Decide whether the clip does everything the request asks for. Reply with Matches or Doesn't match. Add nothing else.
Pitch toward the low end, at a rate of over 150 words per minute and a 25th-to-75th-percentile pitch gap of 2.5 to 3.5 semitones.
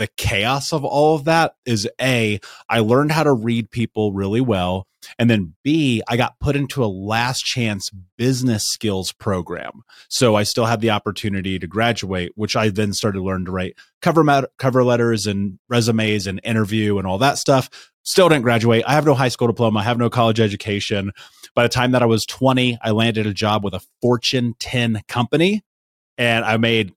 Matches